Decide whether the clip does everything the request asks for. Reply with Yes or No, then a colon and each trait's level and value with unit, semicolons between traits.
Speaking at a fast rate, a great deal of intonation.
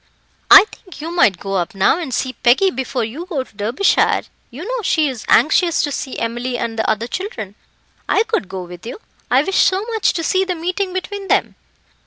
Yes: fast, 210 wpm; wide, 8.5 semitones